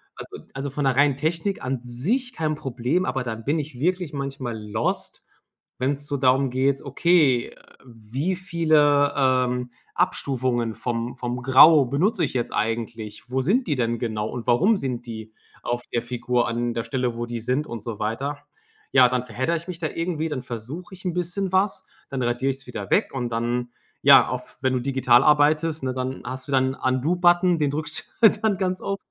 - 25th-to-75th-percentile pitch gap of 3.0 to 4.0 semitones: No, average, 4.5 semitones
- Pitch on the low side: Yes, low, 130 Hz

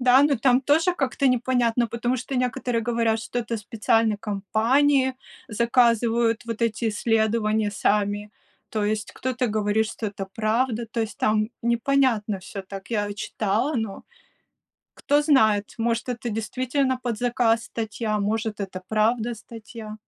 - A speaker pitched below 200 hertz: No, high, 230 Hz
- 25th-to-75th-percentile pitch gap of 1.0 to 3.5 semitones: Yes, narrow, 2.5 semitones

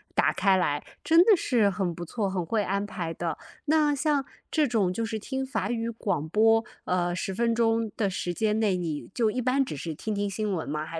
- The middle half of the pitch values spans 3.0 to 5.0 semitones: Yes, average, 4.5 semitones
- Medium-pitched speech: No, high, 210 Hz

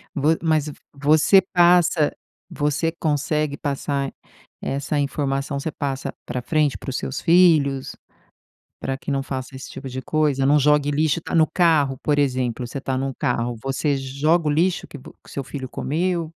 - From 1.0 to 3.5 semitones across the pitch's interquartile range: Yes, narrow, 2.5 semitones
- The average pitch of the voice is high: No, medium, 145 Hz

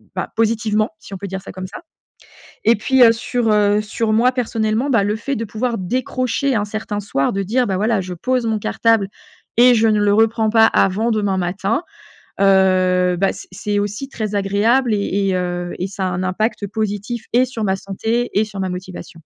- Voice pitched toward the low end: No, high, 210 Hz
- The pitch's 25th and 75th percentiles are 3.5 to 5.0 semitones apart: No, average, 2.9 semitones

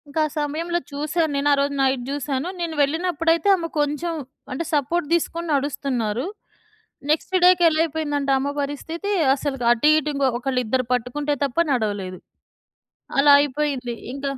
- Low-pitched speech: No, very high, 290 Hz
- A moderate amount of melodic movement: Yes, average, 3.2 semitones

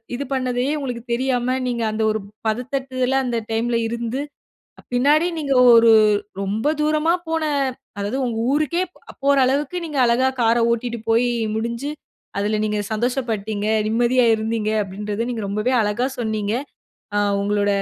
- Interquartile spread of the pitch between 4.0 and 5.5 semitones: No, average, 3.3 semitones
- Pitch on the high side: Yes, high, 235 Hz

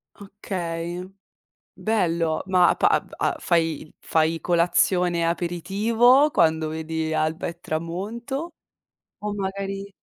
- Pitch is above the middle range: No, medium, 175 Hz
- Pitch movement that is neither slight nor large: Yes, average, 3.4 semitones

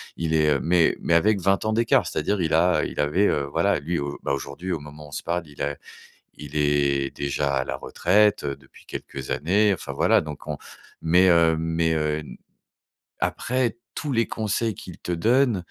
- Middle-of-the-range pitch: No, very low, 80 Hz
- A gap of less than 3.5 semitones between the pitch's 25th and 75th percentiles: No, average, 5.0 semitones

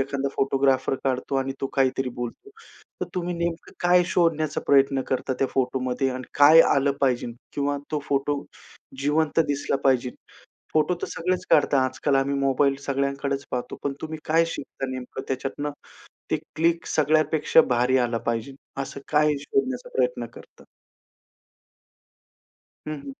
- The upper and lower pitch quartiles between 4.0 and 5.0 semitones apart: No, narrow, 2.5 semitones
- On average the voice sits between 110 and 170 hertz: Yes, medium, 140 Hz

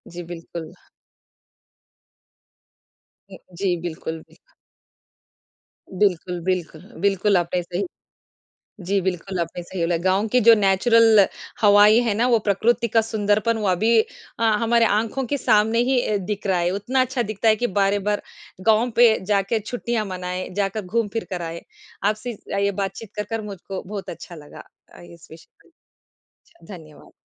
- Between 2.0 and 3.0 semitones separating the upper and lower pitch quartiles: No, average, 3.6 semitones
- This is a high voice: Yes, high, 205 Hz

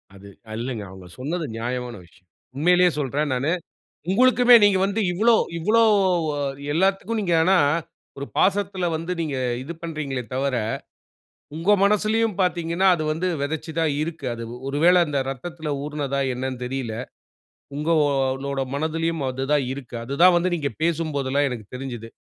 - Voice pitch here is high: No, medium, 155 Hz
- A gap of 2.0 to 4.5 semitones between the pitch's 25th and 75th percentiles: No, average, 5.1 semitones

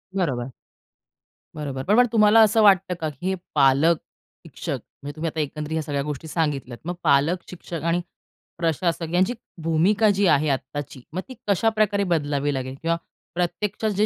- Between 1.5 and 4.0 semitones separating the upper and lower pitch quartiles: No, average, 4.7 semitones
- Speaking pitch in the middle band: Yes, medium, 165 Hz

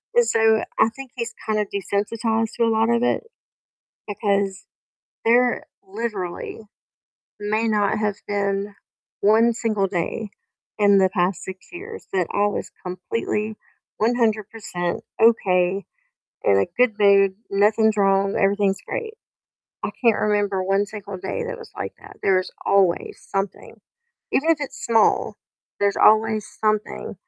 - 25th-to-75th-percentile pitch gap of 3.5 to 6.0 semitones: No, narrow, 2.4 semitones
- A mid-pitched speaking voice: No, high, 210 Hz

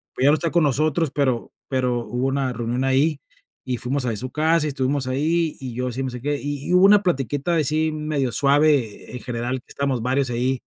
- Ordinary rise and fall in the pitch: Yes, average, 3.2 semitones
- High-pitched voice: No, low, 135 Hz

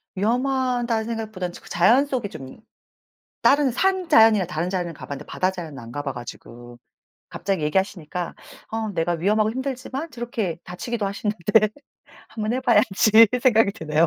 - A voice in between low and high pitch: No, high, 205 Hz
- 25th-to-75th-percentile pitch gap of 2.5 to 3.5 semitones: No, wide, 5.4 semitones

